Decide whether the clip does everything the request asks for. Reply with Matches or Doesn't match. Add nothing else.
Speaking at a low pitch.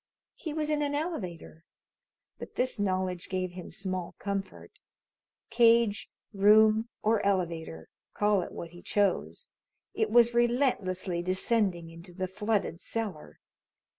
Doesn't match